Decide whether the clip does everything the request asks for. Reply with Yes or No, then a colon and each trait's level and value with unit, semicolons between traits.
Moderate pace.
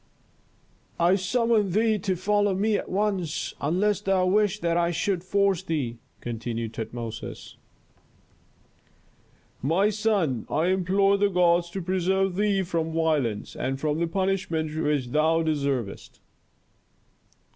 No: slow, 125 wpm